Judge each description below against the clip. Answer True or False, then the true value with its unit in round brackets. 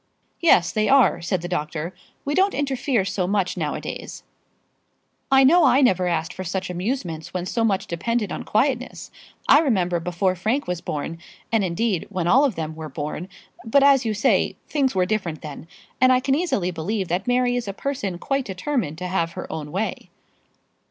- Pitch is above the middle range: True (195 Hz)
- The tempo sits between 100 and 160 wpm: False (190 wpm)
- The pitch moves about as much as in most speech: False (6.6 semitones)